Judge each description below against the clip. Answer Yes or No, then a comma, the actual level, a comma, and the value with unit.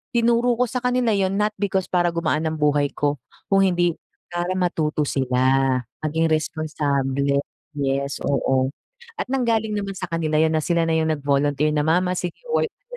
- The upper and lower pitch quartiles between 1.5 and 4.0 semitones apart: No, average, 4.9 semitones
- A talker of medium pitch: Yes, medium, 165 Hz